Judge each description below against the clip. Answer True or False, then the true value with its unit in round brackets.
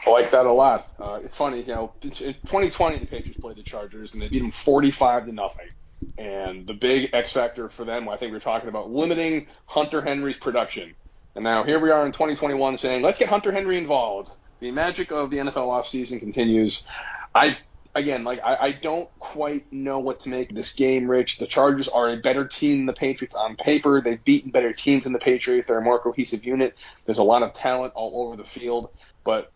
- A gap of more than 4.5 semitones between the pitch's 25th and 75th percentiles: False (3.7 semitones)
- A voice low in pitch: True (130 Hz)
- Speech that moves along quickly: True (220 wpm)